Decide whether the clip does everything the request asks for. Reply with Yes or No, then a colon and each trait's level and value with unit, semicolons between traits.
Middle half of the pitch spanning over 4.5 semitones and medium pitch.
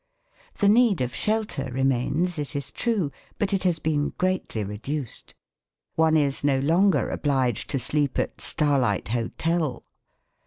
Yes: average, 5.0 semitones; medium, 145 Hz